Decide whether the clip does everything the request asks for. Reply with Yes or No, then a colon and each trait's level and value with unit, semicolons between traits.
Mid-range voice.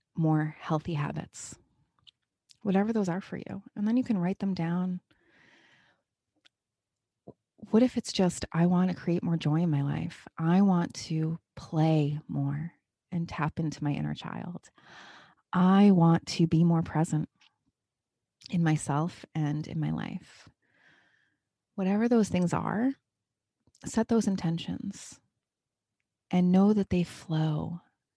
Yes: medium, 170 Hz